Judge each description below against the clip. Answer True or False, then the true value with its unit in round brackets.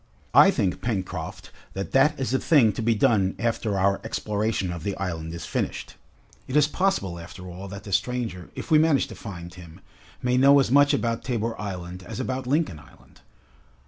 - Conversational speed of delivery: True (190 wpm)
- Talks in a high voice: False (105 Hz)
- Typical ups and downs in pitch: False (5.7 semitones)